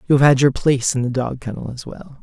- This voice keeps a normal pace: No, fast, 295 wpm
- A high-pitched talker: No, low, 135 Hz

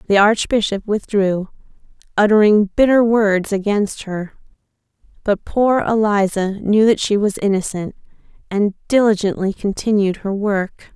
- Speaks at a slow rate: Yes, slow, 115 wpm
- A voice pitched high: Yes, high, 205 Hz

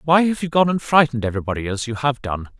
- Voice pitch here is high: No, low, 130 Hz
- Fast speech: Yes, fast, 255 wpm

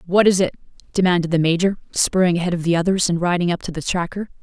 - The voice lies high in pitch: No, medium, 175 Hz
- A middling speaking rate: No, fast, 230 wpm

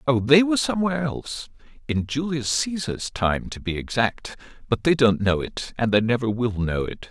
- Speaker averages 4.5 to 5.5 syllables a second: Yes, 5.0 syllables/s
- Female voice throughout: No, male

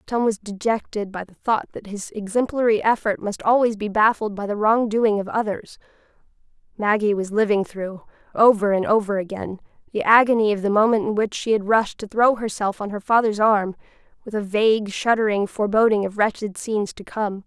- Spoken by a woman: Yes, female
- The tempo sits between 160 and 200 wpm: Yes, average, 190 wpm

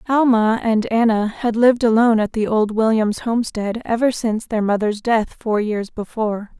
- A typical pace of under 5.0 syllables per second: No, 5.1 syllables/s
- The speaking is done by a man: No, female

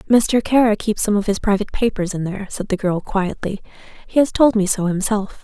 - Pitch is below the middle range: No, high, 205 Hz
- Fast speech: Yes, fast, 220 wpm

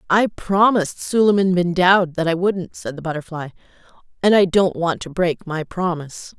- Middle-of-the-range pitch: Yes, medium, 180 Hz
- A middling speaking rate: Yes, average, 180 wpm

